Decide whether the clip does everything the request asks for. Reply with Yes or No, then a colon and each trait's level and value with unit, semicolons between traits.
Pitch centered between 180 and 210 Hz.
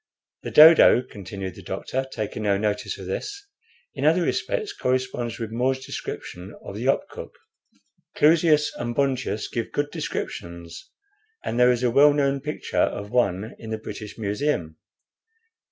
No: low, 120 Hz